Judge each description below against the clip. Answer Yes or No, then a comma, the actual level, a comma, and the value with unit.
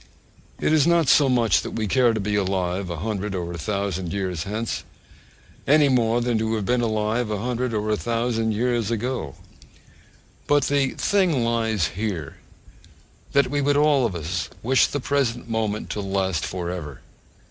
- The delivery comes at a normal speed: Yes, average, 175 wpm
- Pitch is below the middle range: Yes, low, 110 Hz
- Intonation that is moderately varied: Yes, average, 4.2 semitones